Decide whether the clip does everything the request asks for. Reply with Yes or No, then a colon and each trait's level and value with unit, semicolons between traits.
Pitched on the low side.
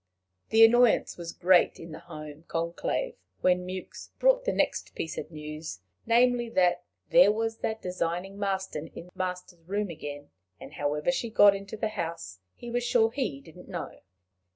No: medium, 185 Hz